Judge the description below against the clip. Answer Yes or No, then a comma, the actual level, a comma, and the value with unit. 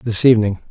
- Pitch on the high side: No, low, 110 Hz